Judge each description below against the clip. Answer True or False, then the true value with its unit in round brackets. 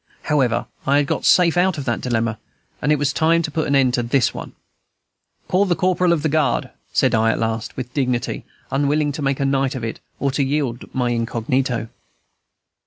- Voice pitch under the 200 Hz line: True (135 Hz)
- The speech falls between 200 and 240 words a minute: True (205 wpm)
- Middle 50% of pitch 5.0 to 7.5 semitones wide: False (3.8 semitones)